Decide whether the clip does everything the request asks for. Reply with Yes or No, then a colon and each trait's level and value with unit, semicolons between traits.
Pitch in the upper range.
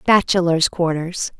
No: medium, 175 Hz